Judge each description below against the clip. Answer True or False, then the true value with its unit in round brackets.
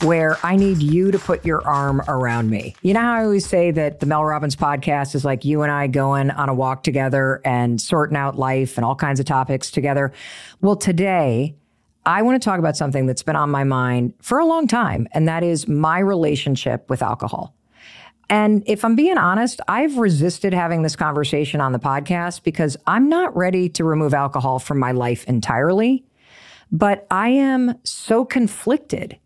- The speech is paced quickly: False (195 wpm)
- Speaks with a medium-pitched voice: True (155 Hz)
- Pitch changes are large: True (6.2 semitones)